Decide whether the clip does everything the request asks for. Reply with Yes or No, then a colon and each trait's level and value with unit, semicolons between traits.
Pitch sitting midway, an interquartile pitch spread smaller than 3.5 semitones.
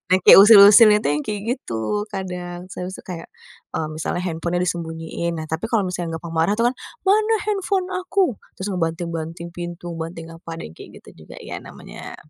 No: medium, 175 Hz; average, 4.0 semitones